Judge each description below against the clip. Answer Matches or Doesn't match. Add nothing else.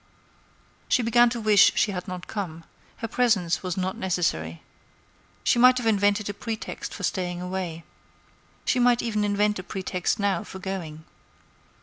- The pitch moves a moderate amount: Matches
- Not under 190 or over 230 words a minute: Doesn't match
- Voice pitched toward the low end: Doesn't match